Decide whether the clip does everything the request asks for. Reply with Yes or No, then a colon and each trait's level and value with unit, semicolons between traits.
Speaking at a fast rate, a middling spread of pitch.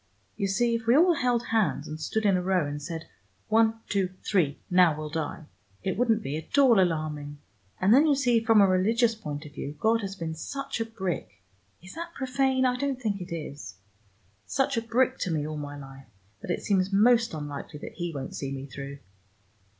No: fast, 210 wpm; wide, 7.2 semitones